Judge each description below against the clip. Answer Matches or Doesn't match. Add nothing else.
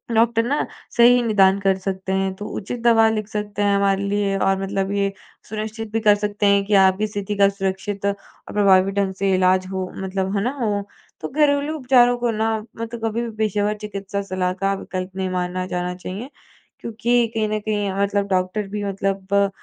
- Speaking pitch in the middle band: Doesn't match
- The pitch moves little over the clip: Matches